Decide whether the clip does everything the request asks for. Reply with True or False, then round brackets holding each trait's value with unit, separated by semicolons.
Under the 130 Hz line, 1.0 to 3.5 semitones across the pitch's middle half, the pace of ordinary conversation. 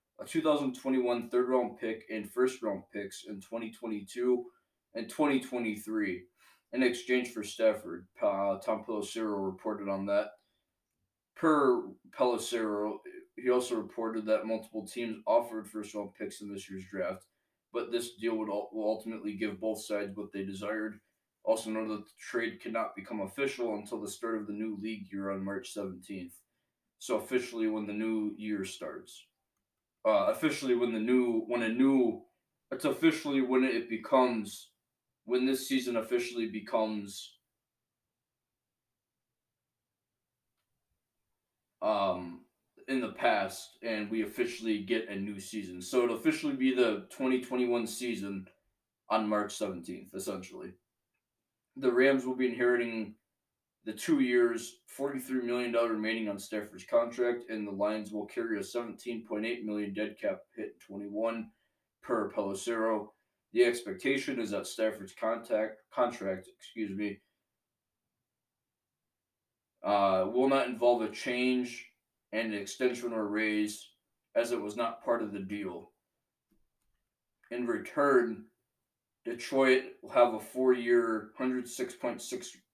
False (115 Hz; 3.0 semitones; 130 wpm)